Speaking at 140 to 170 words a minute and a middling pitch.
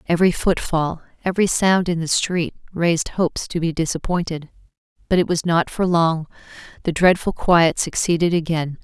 Yes: average, 155 wpm; medium, 170 Hz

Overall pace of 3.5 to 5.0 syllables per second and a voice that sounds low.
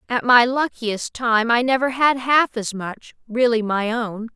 No: 4.0 syllables/s; high, 235 Hz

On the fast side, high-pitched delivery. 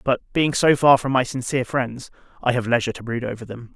No: fast, 240 wpm; low, 125 Hz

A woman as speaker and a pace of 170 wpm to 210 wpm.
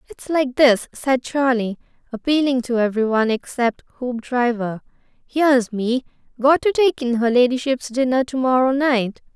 No: female; average, 140 wpm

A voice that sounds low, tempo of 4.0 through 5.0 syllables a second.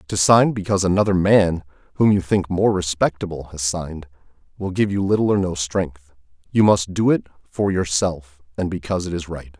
No: very low, 90 Hz; 5.3 syllables/s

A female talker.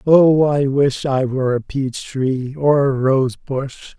No: male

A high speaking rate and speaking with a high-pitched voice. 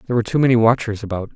No: fast, 265 wpm; low, 115 Hz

